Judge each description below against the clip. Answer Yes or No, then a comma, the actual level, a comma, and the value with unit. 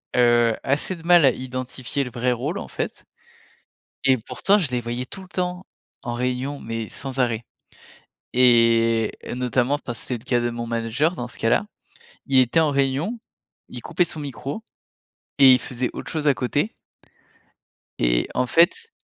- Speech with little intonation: No, average, 3.6 semitones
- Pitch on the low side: Yes, low, 130 Hz